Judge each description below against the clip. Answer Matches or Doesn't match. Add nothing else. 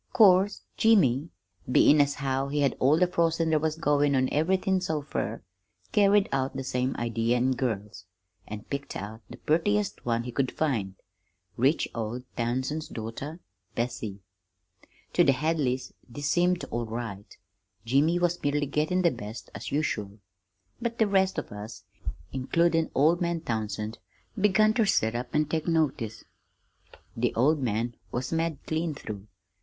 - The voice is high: Doesn't match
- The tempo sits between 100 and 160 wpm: Matches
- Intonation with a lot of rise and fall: Matches